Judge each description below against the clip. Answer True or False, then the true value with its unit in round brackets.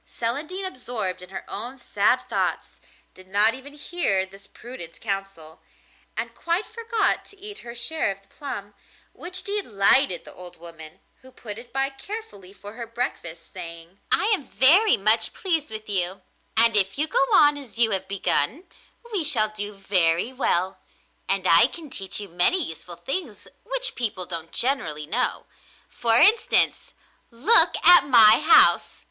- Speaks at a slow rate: False (160 wpm)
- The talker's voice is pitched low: False (225 Hz)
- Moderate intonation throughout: False (7.2 semitones)